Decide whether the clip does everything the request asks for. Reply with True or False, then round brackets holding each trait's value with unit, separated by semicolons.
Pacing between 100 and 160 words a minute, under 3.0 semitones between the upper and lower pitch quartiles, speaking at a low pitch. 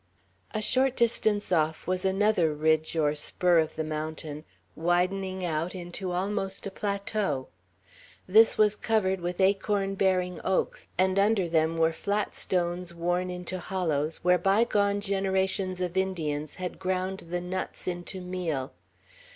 False (140 wpm; 2.6 semitones; 185 Hz)